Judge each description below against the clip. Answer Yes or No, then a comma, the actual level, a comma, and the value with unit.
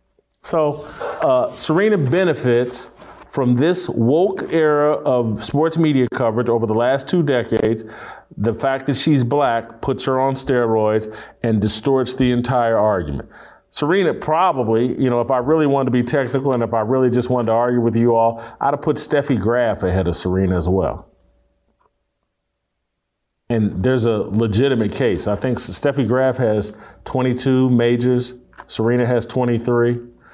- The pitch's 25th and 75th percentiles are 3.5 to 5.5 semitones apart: No, average, 2.9 semitones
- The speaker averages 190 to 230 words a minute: No, average, 155 wpm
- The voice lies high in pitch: No, low, 125 Hz